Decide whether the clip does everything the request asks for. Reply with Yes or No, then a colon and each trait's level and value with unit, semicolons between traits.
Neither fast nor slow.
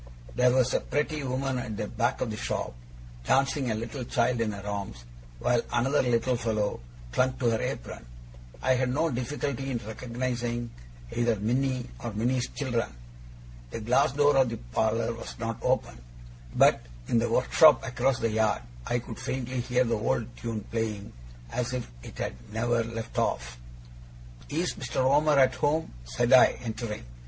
Yes: average, 165 wpm